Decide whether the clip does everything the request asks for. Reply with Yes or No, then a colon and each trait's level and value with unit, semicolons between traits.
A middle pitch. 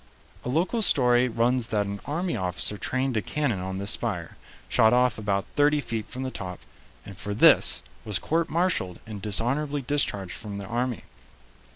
No: low, 115 Hz